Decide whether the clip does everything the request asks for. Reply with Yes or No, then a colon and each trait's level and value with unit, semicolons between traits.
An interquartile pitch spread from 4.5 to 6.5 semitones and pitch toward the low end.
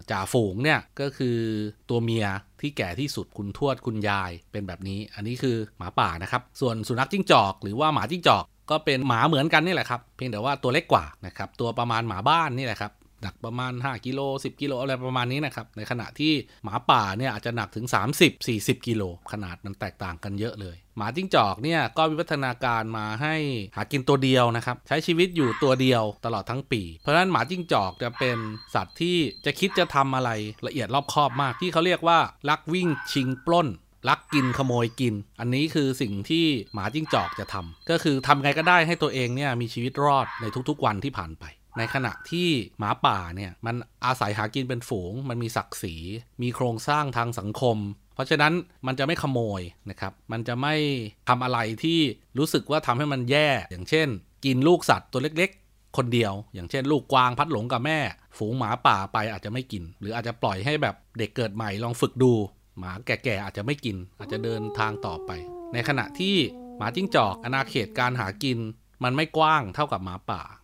Yes: average, 5.1 semitones; low, 125 Hz